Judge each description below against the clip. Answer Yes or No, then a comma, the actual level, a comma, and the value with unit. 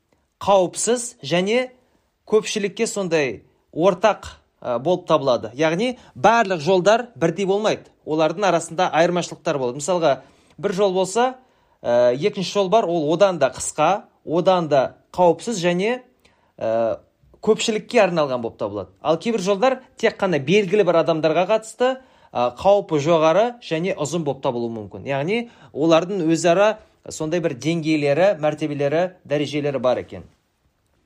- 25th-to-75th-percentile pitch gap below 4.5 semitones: No, average, 5.1 semitones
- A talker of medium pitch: Yes, medium, 175 Hz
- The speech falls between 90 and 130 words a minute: Yes, average, 120 wpm